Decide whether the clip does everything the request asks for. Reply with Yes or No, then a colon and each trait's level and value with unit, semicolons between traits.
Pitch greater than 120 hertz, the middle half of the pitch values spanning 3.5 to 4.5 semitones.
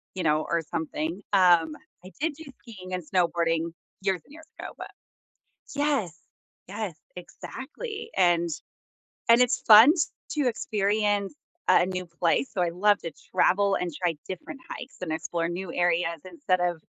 Yes: medium, 185 Hz; average, 3.8 semitones